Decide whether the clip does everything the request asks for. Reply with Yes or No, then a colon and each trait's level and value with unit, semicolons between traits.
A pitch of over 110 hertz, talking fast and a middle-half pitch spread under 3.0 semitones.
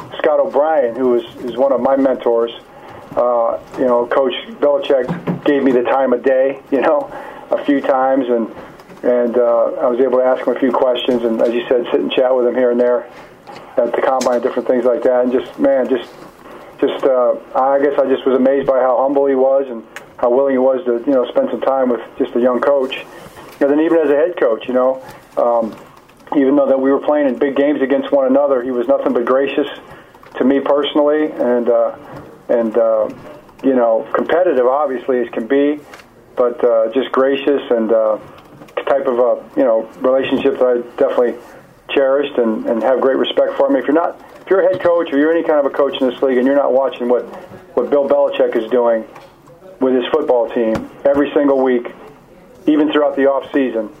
Yes: low, 135 Hz; fast, 220 wpm; narrow, 2.6 semitones